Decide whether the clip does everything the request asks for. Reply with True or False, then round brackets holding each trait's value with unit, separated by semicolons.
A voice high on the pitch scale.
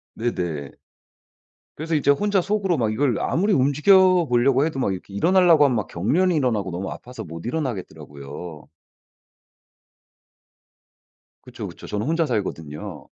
False (125 Hz)